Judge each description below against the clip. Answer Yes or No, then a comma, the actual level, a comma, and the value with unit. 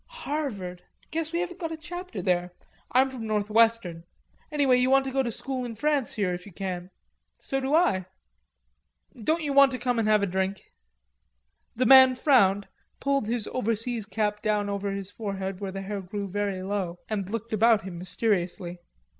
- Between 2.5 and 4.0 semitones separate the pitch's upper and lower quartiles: No, wide, 5.4 semitones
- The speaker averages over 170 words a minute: Yes, average, 185 wpm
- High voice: Yes, high, 215 Hz